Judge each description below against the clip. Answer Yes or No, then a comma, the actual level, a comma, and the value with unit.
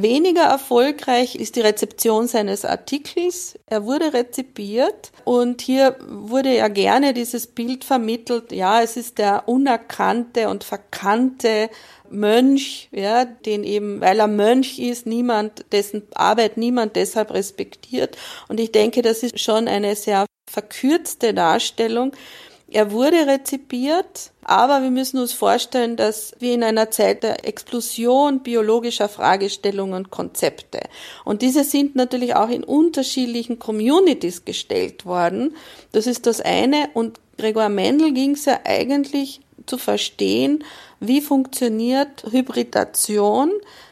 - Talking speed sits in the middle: No, slow, 130 wpm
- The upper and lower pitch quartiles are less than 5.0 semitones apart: Yes, average, 3.7 semitones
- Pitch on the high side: Yes, high, 240 Hz